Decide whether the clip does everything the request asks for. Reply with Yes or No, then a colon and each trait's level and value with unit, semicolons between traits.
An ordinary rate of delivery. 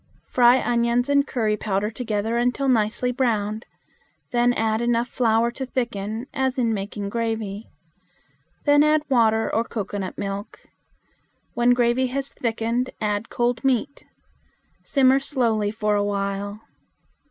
No: slow, 130 wpm